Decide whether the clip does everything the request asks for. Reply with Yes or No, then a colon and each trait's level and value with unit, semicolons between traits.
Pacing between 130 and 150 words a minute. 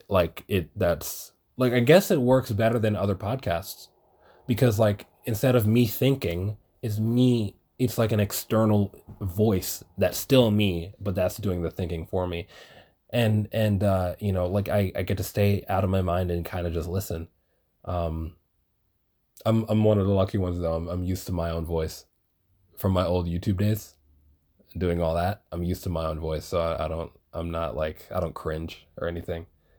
No: average, 195 wpm